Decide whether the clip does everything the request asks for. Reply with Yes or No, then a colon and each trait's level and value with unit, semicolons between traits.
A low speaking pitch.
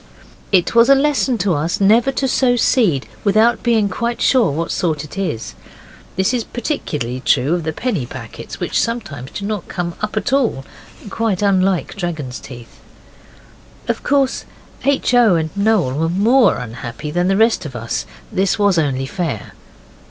No: high, 190 Hz